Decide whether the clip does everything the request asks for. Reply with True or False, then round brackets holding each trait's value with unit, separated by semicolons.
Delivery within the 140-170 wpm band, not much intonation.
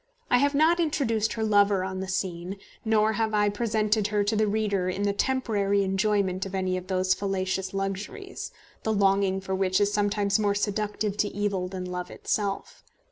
False (185 wpm; 2.1 semitones)